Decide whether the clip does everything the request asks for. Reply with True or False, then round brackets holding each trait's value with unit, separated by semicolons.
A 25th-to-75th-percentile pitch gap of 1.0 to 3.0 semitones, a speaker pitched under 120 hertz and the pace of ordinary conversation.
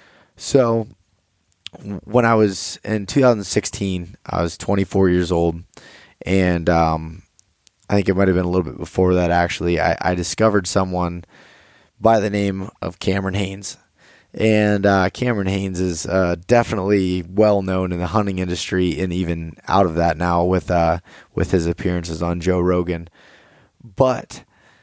True (2.5 semitones; 95 Hz; 150 wpm)